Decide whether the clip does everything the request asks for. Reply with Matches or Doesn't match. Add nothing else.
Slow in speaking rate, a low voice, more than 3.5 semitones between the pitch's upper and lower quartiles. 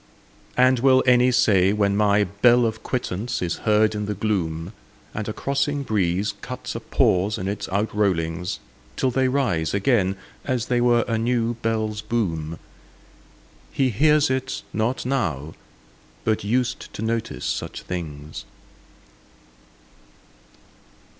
Matches